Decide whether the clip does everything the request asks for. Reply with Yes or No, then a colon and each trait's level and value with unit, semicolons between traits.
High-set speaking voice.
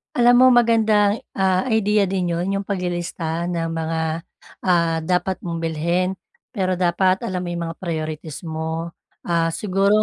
No: medium, 180 Hz